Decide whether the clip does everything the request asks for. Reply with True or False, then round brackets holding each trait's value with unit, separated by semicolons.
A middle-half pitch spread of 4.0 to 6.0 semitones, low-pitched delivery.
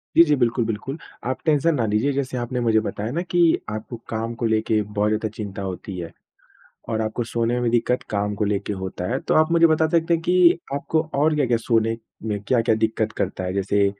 True (4.8 semitones; 115 Hz)